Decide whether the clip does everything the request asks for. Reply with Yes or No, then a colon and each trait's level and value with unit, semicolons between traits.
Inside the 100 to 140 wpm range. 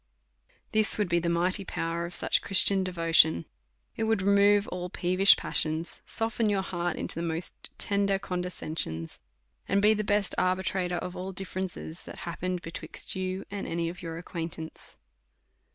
No: average, 155 wpm